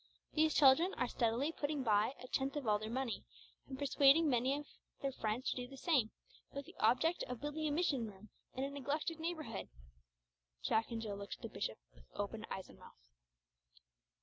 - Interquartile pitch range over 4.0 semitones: Yes, average, 4.4 semitones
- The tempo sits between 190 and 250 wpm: Yes, average, 195 wpm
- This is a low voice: No, very high, 265 Hz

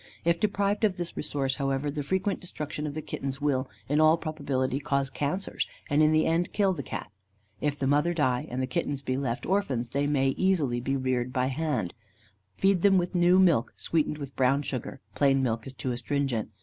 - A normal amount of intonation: Yes, average, 4.2 semitones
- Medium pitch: Yes, medium, 145 Hz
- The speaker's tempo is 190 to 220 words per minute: Yes, average, 200 wpm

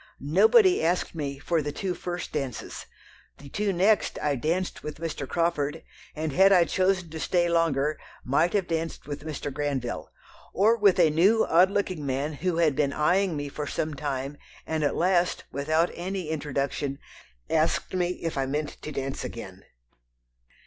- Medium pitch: Yes, medium, 160 Hz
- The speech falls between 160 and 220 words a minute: Yes, average, 170 wpm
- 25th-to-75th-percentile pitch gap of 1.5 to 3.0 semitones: No, average, 3.8 semitones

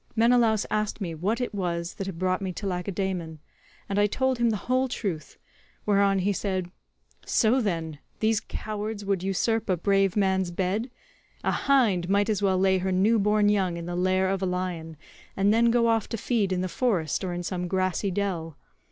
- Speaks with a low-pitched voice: No, high, 195 Hz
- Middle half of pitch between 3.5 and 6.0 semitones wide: No, average, 2.9 semitones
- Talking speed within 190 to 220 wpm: Yes, average, 195 wpm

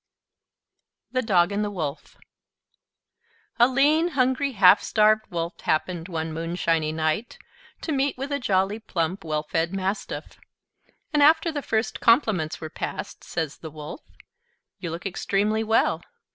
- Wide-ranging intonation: Yes, wide, 6.9 semitones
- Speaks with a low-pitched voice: No, high, 195 Hz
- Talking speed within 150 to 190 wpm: No, average, 140 wpm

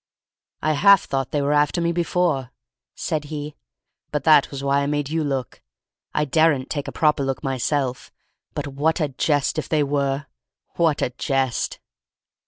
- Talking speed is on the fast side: No, average, 165 wpm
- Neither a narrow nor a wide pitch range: No, narrow, 2.3 semitones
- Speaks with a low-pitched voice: No, medium, 145 Hz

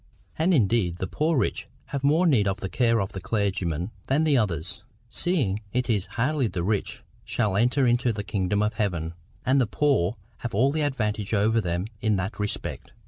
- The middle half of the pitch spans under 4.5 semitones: No, average, 5.2 semitones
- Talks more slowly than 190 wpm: No, average, 195 wpm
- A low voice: Yes, low, 110 Hz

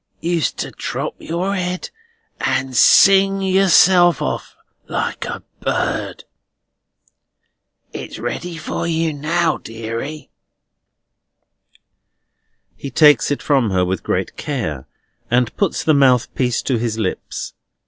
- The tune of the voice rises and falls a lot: Yes, wide, 6.4 semitones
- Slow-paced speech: Yes, slow, 110 wpm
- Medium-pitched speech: Yes, medium, 150 Hz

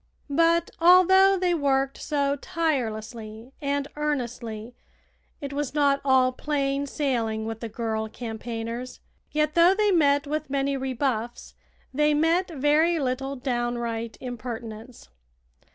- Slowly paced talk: Yes, slow, 120 wpm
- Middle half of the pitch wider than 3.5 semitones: Yes, average, 4.1 semitones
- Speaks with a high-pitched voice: Yes, very high, 275 Hz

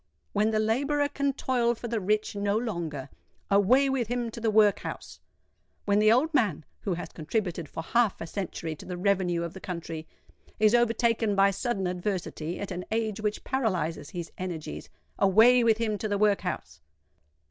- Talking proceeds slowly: No, average, 175 wpm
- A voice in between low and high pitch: No, high, 210 Hz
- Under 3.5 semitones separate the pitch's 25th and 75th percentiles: No, average, 4.3 semitones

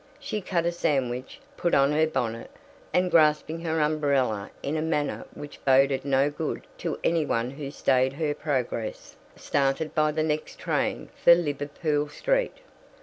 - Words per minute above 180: No, average, 155 wpm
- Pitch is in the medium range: Yes, medium, 150 Hz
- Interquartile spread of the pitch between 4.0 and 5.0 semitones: No, average, 2.8 semitones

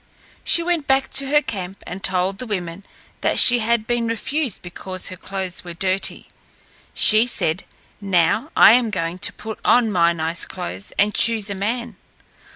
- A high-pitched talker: Yes, high, 200 Hz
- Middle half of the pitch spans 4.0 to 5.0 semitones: Yes, average, 4.5 semitones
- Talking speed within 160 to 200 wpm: Yes, average, 170 wpm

